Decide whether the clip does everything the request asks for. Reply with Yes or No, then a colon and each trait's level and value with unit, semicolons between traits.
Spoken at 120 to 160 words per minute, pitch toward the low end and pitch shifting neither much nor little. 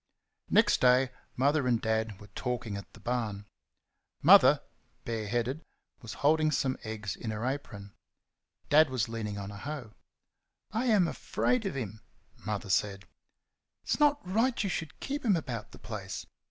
No: average, 155 wpm; low, 120 Hz; wide, 6.3 semitones